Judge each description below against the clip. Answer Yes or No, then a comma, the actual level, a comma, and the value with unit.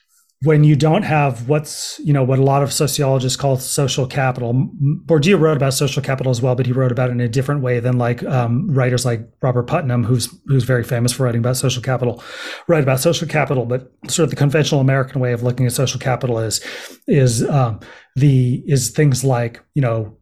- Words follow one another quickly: Yes, fast, 215 wpm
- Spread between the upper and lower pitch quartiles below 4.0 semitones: Yes, narrow, 2.5 semitones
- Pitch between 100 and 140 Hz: Yes, low, 130 Hz